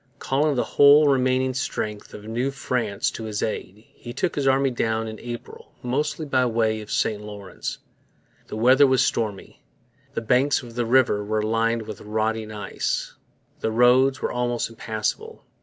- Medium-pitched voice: No, low, 120 Hz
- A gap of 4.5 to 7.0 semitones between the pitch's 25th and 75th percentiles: No, average, 3.3 semitones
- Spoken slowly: No, average, 170 wpm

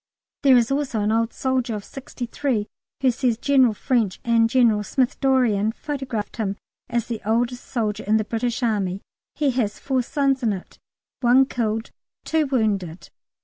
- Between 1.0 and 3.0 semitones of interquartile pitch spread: No, average, 3.4 semitones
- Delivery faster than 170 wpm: No, average, 165 wpm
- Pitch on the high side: Yes, high, 235 Hz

